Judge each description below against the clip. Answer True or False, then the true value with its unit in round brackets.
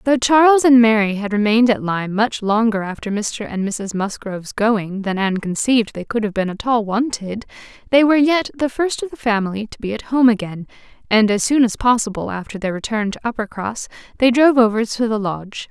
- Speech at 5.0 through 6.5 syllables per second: True (5.7 syllables/s)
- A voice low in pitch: False (220 Hz)